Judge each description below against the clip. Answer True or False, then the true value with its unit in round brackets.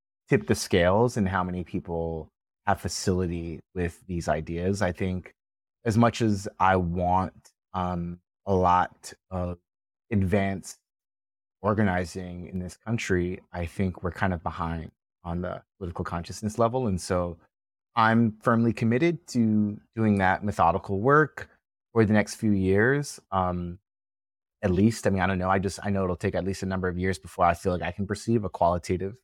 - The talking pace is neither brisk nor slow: True (170 wpm)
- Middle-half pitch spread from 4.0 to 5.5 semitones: False (2.8 semitones)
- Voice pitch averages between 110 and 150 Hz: False (95 Hz)